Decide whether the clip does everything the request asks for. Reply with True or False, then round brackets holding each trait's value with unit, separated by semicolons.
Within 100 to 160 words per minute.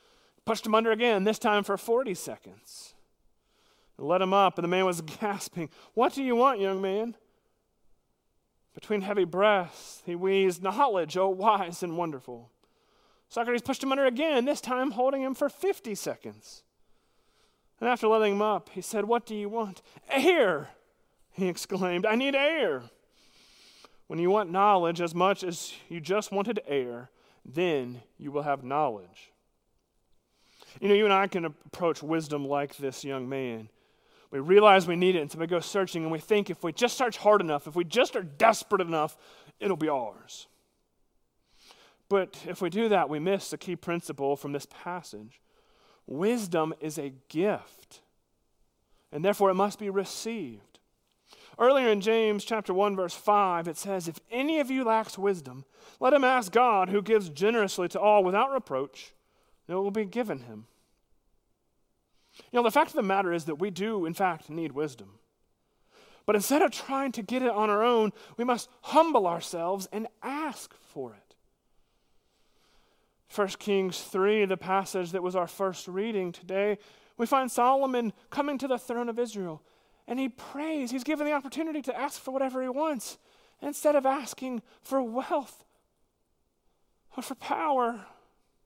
False (170 wpm)